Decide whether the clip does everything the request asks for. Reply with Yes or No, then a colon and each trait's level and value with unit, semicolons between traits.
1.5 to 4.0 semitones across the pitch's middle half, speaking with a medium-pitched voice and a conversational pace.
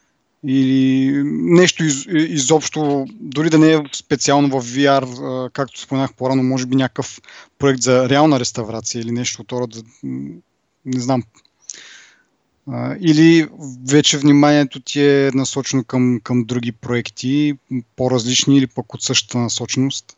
No: narrow, 2.4 semitones; low, 130 Hz; average, 130 wpm